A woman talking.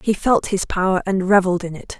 Yes: female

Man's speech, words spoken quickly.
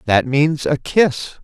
No: male; average, 165 wpm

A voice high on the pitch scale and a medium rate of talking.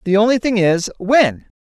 Yes: high, 210 Hz; average, 185 wpm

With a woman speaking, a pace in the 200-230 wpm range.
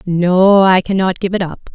Yes: female; fast, 205 wpm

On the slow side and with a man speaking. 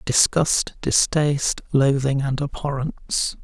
Yes: slow, 85 wpm; male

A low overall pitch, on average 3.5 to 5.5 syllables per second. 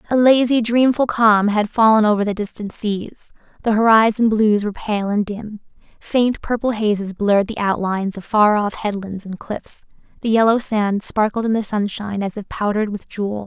No: high, 215 Hz; 5.1 syllables/s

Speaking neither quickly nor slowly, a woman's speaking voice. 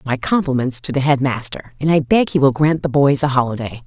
No: fast, 250 wpm; female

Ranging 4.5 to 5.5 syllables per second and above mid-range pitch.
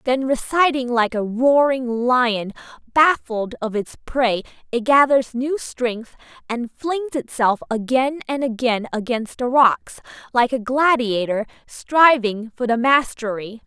No: 3.7 syllables/s; high, 245 Hz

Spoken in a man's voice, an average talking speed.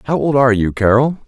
No: male; fast, 235 wpm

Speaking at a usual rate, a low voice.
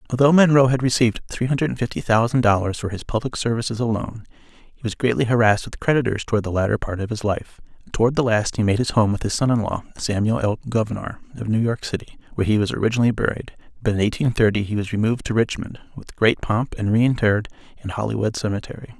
No: fast, 220 wpm; low, 115 Hz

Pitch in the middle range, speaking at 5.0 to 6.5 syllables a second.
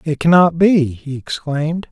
No: medium, 155 Hz; 4.4 syllables/s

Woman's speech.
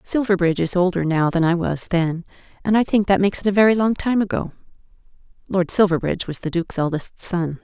Yes: female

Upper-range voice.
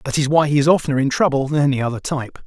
No: medium, 140 Hz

